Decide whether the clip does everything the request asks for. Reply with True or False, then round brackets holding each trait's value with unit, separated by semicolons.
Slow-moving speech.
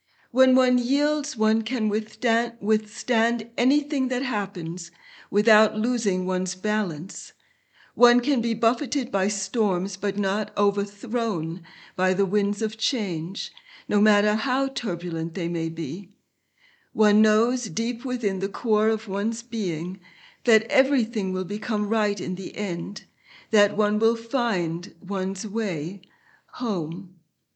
True (125 wpm)